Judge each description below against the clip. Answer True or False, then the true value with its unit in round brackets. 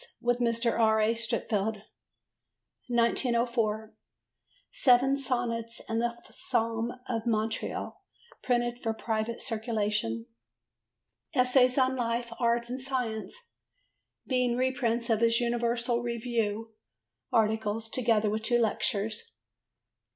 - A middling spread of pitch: False (1.7 semitones)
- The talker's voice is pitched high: True (235 Hz)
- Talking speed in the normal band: False (100 wpm)